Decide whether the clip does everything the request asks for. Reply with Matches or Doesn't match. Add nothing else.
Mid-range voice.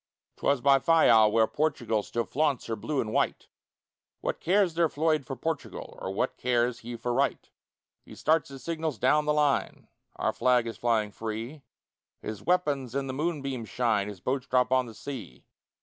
Doesn't match